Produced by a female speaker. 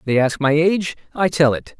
No: male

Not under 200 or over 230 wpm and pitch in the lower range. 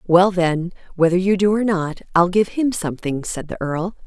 No: fast, 205 wpm; medium, 180 Hz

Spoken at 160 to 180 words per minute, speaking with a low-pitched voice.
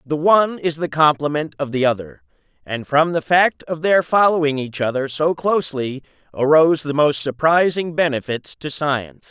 No: average, 170 wpm; medium, 150 Hz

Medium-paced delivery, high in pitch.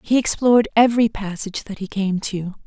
Yes: average, 180 wpm; high, 210 Hz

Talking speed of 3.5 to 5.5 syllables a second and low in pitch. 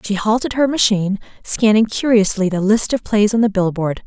No: 5.4 syllables/s; high, 210 Hz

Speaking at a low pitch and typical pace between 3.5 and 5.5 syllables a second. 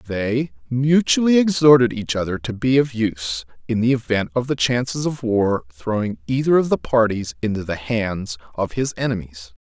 Yes: low, 115 Hz; 4.8 syllables/s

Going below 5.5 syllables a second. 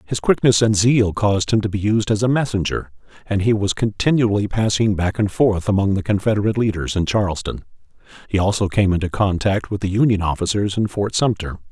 No: 5.8 syllables/s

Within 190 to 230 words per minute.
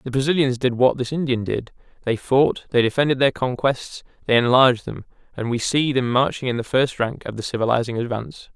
Yes: fast, 205 wpm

